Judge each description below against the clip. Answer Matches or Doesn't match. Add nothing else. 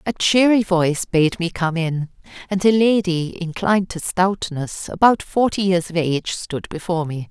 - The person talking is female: Matches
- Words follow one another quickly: Doesn't match